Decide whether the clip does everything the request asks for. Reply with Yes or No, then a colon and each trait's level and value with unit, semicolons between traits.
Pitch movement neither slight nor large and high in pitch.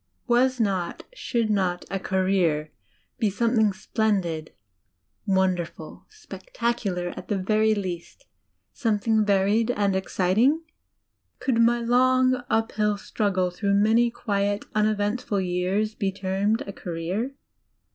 Yes: average, 3.4 semitones; high, 205 Hz